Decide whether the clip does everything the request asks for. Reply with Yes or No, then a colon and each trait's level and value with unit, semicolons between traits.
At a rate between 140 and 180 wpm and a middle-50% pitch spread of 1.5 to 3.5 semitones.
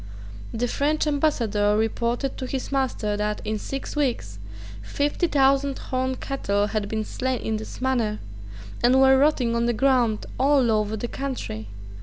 No: average, 155 wpm; average, 4.0 semitones